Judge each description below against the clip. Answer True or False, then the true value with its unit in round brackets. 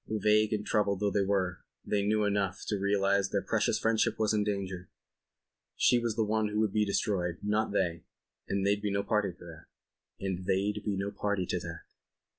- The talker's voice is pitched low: True (100 Hz)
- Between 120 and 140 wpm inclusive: False (155 wpm)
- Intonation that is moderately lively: False (1.7 semitones)